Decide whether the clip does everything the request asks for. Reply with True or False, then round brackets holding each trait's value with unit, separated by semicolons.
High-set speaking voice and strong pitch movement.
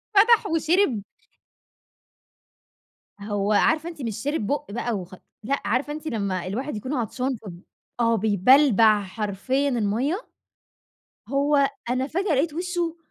True (255 Hz; 6.1 semitones)